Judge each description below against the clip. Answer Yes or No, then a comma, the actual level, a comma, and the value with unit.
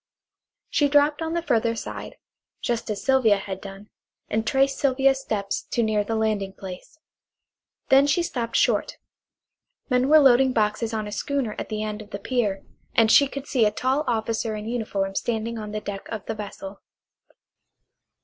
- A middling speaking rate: Yes, average, 175 wpm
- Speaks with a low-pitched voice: No, high, 225 Hz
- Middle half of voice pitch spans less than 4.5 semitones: Yes, average, 4.1 semitones